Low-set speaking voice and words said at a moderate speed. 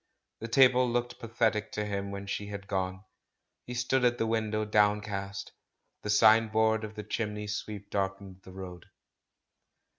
Yes: low, 105 Hz; average, 155 wpm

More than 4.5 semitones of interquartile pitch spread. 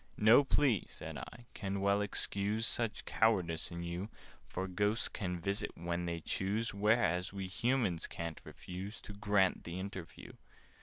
No: average, 3.2 semitones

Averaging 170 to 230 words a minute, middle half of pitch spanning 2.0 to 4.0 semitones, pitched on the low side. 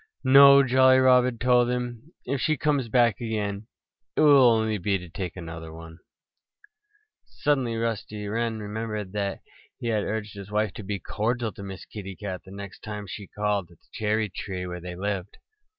Yes: average, 180 wpm; average, 3.6 semitones; low, 105 Hz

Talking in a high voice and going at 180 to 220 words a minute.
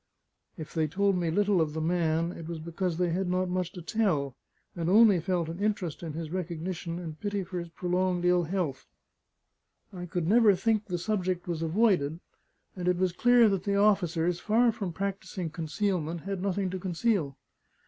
No: medium, 180 Hz; average, 185 wpm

